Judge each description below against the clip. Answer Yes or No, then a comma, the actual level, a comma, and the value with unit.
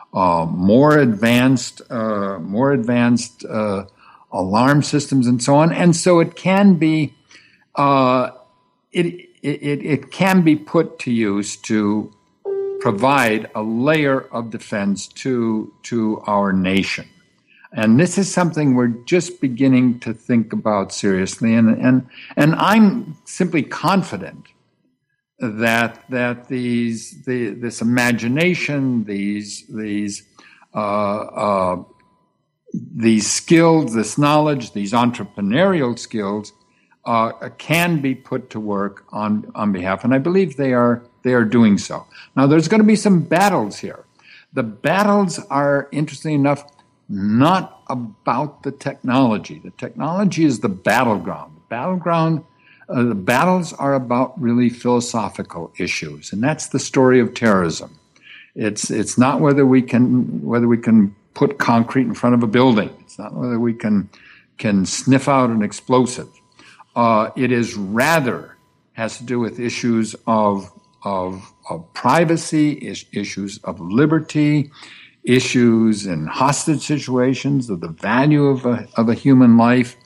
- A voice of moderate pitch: No, low, 125 Hz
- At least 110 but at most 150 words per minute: Yes, slow, 135 wpm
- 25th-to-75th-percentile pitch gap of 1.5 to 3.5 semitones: No, average, 4.7 semitones